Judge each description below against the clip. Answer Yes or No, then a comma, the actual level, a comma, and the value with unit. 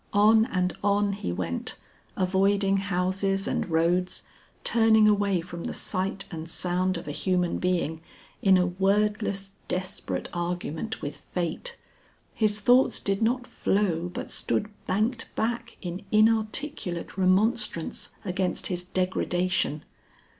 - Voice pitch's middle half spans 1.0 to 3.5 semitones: Yes, average, 2.9 semitones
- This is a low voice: No, high, 190 Hz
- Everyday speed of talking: No, slow, 125 wpm